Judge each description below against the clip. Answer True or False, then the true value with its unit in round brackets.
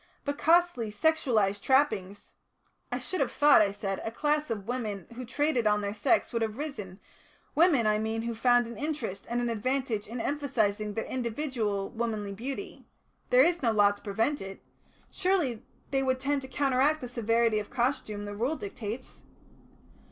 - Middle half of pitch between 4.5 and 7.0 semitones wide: True (4.8 semitones)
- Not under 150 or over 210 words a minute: True (175 wpm)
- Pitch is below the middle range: False (235 Hz)